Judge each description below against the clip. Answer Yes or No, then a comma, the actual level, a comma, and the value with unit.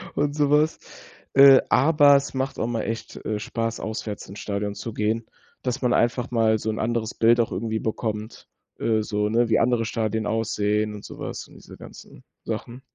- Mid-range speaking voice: No, low, 115 Hz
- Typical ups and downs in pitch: No, narrow, 2.3 semitones